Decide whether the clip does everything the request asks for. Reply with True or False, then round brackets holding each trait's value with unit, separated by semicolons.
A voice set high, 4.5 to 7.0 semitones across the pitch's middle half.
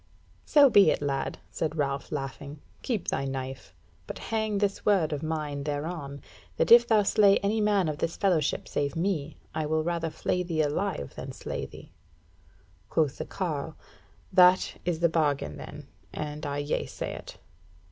False (160 Hz; 4.9 semitones)